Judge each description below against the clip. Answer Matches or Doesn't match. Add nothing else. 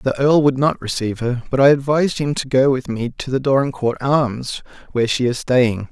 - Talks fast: Matches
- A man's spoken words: Matches